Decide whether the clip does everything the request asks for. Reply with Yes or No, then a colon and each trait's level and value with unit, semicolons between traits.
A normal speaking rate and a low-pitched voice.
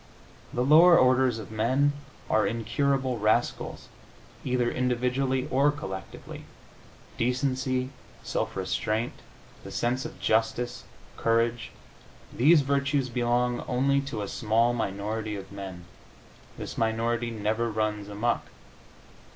No: slow, 110 wpm; low, 120 Hz